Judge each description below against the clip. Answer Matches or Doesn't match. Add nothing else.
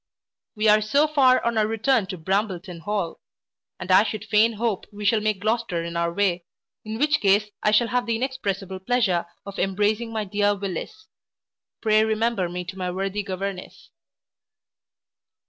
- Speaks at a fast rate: Doesn't match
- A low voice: Doesn't match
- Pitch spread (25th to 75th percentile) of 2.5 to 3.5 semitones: Matches